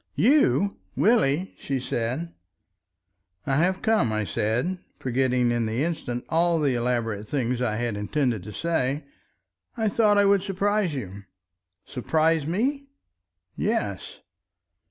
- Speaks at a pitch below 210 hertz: Yes, medium, 140 Hz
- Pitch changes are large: Yes, wide, 7.6 semitones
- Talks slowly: Yes, slow, 120 wpm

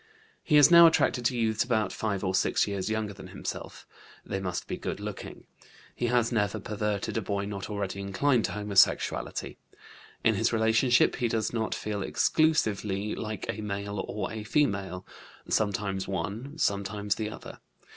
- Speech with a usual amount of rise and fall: No, narrow, 2.3 semitones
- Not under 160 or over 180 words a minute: Yes, average, 165 wpm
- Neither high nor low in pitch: No, low, 105 Hz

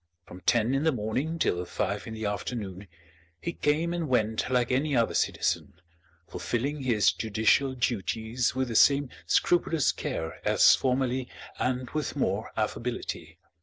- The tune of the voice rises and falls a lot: No, average, 4.0 semitones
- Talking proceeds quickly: No, average, 145 wpm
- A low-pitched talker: Yes, low, 125 Hz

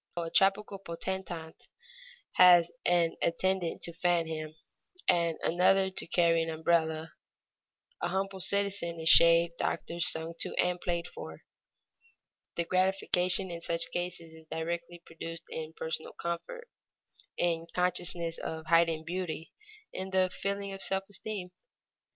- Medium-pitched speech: Yes, medium, 170 Hz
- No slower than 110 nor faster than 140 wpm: Yes, slow, 135 wpm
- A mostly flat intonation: Yes, narrow, 2.1 semitones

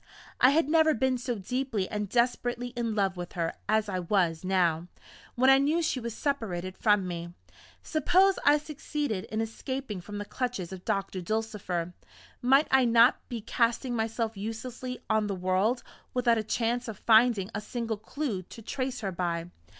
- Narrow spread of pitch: No, average, 4.8 semitones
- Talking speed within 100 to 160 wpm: No, average, 175 wpm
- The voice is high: Yes, high, 225 Hz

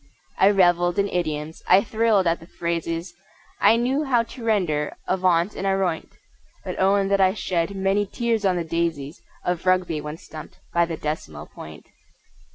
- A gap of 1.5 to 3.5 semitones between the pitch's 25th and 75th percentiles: Yes, average, 3.2 semitones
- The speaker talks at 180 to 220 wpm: No, average, 165 wpm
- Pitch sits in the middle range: Yes, medium, 180 Hz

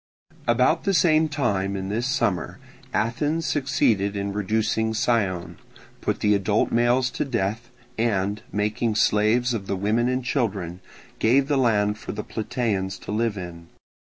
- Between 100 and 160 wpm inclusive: Yes, average, 150 wpm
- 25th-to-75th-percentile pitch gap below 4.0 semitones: Yes, average, 3.5 semitones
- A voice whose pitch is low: Yes, low, 110 Hz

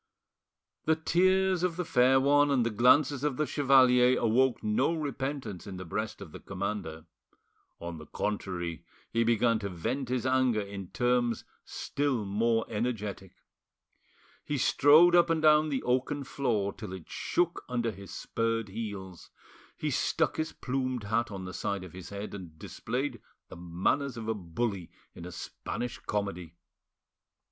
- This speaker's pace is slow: No, average, 155 wpm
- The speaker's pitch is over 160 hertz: No, low, 115 Hz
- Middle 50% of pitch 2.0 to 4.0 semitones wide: No, wide, 5.4 semitones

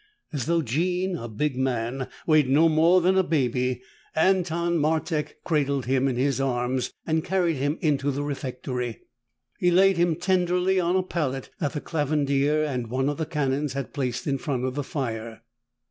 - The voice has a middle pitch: Yes, medium, 145 Hz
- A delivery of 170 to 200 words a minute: Yes, average, 175 wpm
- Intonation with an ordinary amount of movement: Yes, average, 4.3 semitones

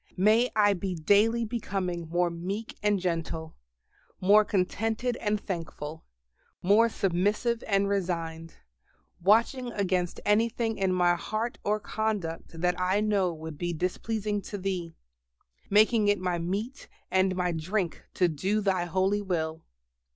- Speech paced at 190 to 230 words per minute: No, slow, 135 wpm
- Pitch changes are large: No, average, 3.4 semitones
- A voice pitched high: Yes, high, 195 Hz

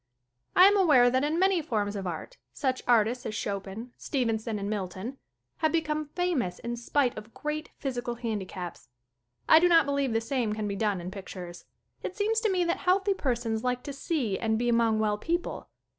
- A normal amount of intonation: No, wide, 6.2 semitones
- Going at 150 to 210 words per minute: Yes, average, 195 wpm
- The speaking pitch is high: Yes, high, 245 Hz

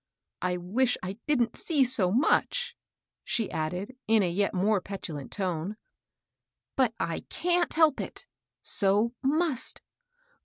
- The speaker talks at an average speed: No, slow, 125 wpm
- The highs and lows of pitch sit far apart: Yes, wide, 6.2 semitones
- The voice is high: Yes, high, 215 Hz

